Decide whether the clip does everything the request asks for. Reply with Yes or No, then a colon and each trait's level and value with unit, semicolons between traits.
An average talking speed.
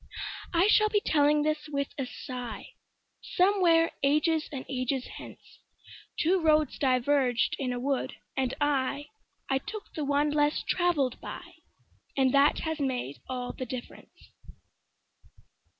No: slow, 120 wpm